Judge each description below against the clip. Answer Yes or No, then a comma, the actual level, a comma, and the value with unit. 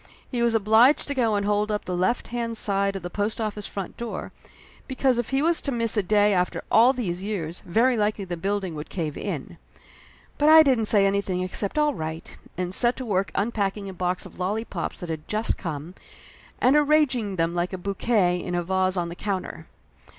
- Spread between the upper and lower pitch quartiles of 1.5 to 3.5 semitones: No, average, 4.4 semitones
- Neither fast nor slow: No, fast, 210 wpm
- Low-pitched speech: No, high, 205 Hz